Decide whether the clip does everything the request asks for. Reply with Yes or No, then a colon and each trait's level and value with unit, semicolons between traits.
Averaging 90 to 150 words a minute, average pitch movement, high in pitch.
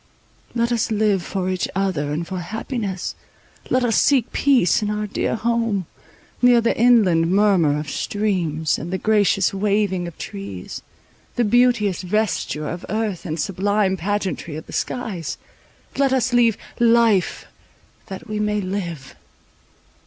Yes: average, 145 wpm; average, 4.3 semitones; high, 205 Hz